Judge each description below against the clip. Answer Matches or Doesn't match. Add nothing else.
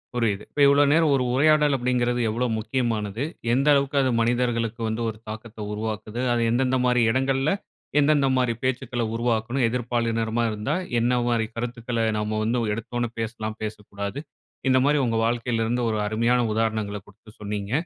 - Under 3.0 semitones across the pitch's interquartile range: Matches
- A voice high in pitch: Doesn't match